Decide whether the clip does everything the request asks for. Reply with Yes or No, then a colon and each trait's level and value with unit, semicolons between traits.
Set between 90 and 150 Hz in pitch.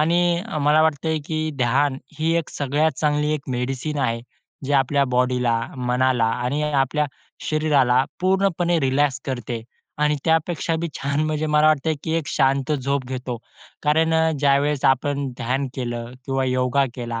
Yes: medium, 140 Hz